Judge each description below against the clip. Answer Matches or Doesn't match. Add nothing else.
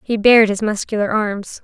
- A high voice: Matches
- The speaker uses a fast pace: Doesn't match